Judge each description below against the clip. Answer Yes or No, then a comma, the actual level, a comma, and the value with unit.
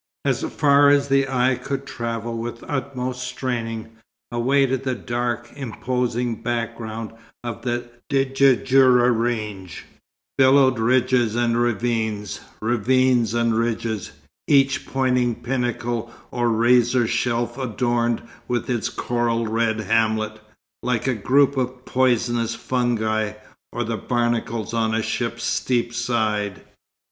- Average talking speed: No, slow, 115 wpm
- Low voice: Yes, low, 120 Hz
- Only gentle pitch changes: Yes, narrow, 2.0 semitones